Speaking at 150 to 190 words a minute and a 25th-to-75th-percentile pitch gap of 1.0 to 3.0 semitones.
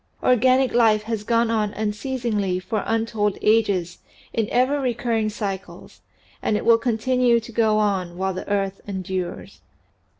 No: average, 140 wpm; average, 2.7 semitones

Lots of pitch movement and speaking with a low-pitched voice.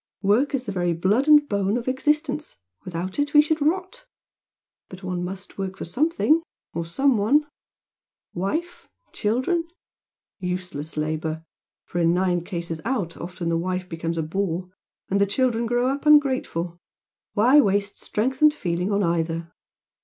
No: wide, 7.8 semitones; high, 200 Hz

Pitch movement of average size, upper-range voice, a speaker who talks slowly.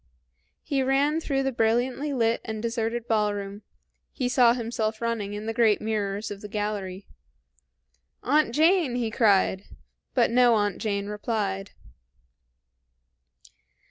Yes: average, 3.1 semitones; high, 225 Hz; slow, 125 wpm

